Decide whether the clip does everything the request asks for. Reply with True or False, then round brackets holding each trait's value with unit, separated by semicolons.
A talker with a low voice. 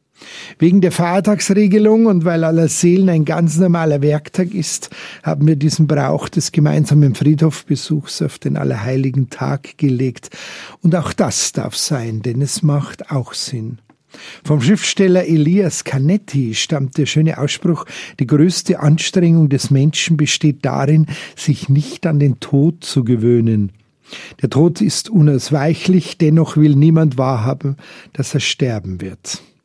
False (150 Hz)